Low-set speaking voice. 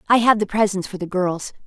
No: high, 195 Hz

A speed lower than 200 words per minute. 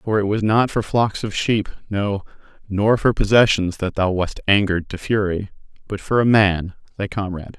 Yes: average, 190 wpm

